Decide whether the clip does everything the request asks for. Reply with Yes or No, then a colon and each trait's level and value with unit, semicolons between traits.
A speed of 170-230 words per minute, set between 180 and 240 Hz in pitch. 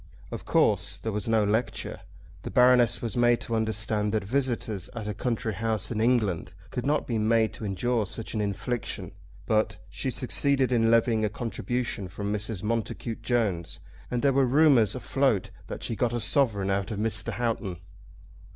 No: average, 175 wpm; low, 115 Hz